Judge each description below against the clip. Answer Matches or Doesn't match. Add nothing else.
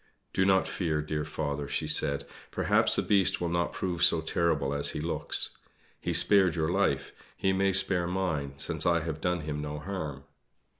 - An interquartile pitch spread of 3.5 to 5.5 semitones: Matches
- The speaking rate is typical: Matches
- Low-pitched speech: Matches